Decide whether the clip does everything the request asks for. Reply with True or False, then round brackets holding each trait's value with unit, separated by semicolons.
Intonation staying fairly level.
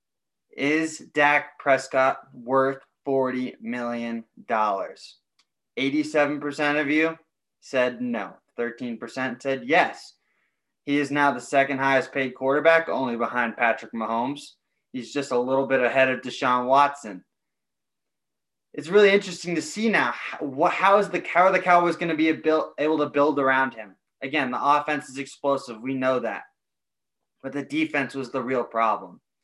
False (3.0 semitones)